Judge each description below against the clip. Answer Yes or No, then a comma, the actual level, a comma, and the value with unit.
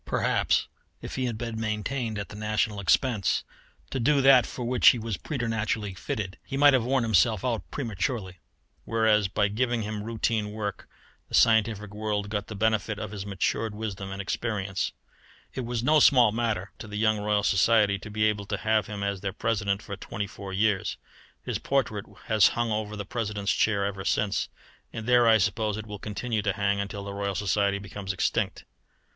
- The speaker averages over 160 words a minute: Yes, average, 190 wpm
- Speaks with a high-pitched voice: No, low, 105 Hz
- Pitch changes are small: Yes, narrow, 2.1 semitones